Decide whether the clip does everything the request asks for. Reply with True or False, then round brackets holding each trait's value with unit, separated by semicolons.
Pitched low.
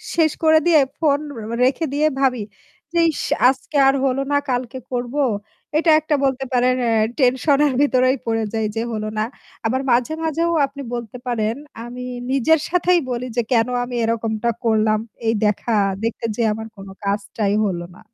False (250 Hz)